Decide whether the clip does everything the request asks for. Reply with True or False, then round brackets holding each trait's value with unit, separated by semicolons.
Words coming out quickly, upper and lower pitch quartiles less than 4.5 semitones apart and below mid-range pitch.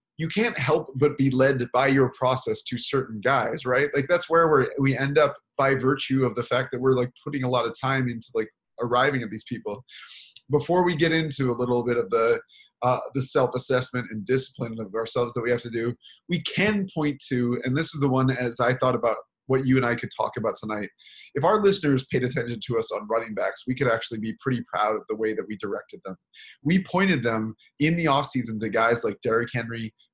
True (230 wpm; 2.9 semitones; 130 Hz)